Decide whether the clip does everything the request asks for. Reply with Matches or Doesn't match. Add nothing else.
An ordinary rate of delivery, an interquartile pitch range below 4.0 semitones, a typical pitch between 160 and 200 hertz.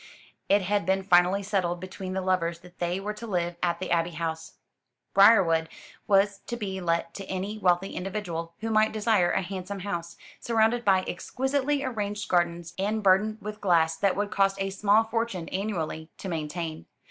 Matches